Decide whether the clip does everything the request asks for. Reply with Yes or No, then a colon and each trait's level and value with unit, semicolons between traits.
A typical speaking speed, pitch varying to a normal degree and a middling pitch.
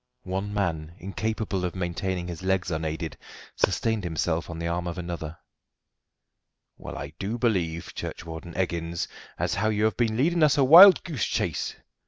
No: average, 160 wpm; average, 4.5 semitones; very low, 90 Hz